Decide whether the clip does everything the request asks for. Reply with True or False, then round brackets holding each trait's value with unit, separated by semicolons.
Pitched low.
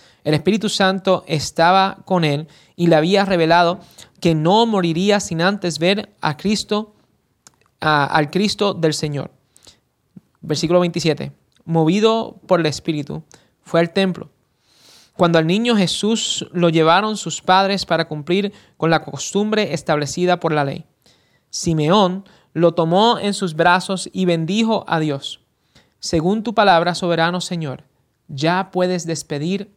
False (175 Hz)